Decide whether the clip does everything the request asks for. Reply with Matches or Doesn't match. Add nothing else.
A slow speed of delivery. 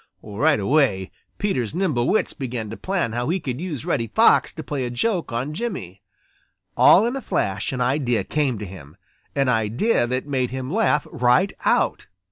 Doesn't match